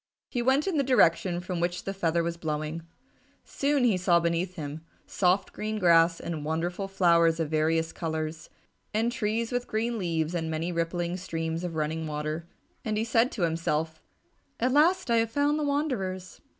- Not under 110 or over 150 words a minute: No, average, 175 wpm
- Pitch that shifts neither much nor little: No, wide, 5.7 semitones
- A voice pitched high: No, medium, 175 Hz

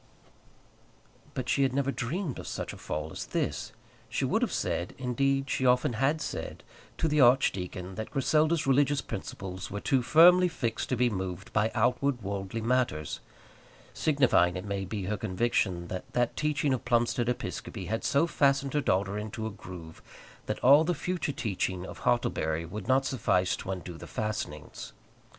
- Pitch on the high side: No, low, 120 Hz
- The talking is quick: No, average, 170 wpm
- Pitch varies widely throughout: Yes, wide, 6.5 semitones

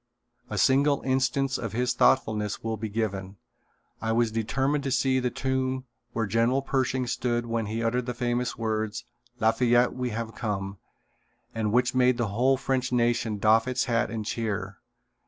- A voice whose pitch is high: No, low, 120 Hz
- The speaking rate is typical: Yes, average, 165 wpm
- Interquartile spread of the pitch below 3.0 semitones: Yes, narrow, 2.5 semitones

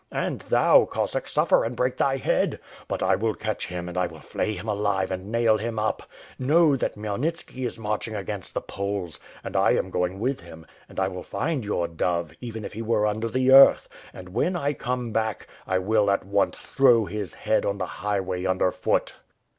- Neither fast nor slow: No, fast, 210 wpm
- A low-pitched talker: Yes, low, 105 Hz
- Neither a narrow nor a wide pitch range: Yes, average, 4.1 semitones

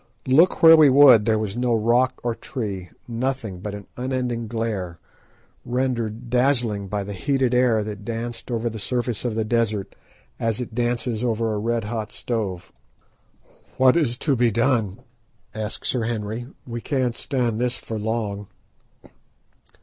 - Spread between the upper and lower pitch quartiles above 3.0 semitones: No, narrow, 2.6 semitones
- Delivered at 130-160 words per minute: Yes, average, 155 wpm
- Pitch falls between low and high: No, low, 115 Hz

